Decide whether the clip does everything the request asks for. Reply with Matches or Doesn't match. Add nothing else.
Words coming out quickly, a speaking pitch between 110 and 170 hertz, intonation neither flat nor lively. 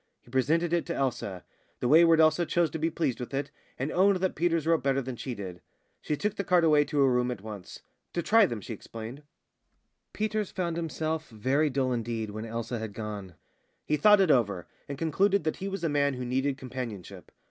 Doesn't match